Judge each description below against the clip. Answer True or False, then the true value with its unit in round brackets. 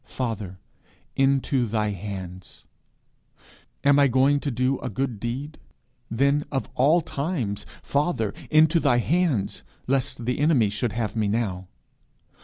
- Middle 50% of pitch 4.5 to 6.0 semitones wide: True (4.9 semitones)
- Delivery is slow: True (130 wpm)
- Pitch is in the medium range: False (125 Hz)